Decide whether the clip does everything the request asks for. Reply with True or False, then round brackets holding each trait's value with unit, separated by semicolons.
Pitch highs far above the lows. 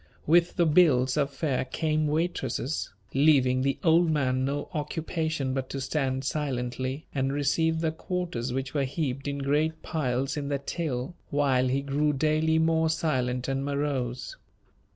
False (3.3 semitones)